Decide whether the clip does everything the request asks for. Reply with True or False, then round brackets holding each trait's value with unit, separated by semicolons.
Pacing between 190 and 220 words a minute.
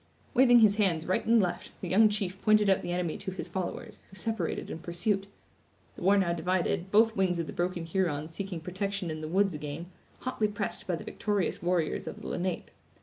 True (205 wpm)